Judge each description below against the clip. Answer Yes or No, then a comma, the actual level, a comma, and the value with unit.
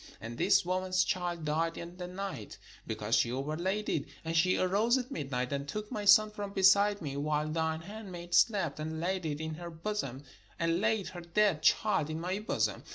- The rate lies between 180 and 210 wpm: Yes, average, 195 wpm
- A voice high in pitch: No, medium, 175 Hz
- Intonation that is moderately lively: Yes, average, 4.2 semitones